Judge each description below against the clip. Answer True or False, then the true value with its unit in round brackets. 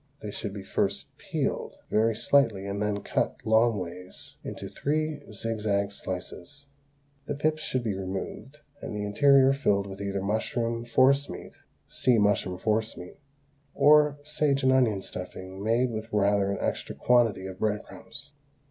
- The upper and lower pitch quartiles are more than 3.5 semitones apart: True (4.8 semitones)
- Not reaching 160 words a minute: True (150 wpm)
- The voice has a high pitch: False (110 Hz)